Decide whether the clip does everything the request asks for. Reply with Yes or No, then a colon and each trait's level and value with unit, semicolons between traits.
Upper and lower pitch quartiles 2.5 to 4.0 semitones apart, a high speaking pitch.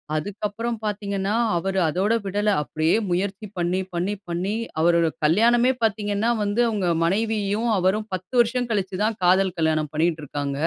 Yes: average, 3.7 semitones; high, 195 Hz